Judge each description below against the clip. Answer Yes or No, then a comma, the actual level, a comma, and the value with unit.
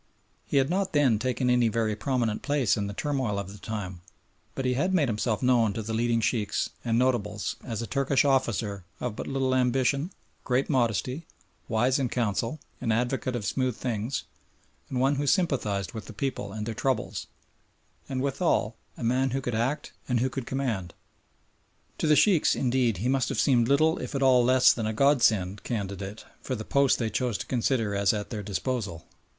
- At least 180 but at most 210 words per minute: Yes, average, 195 wpm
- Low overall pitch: Yes, low, 125 Hz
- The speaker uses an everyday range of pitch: Yes, average, 3.7 semitones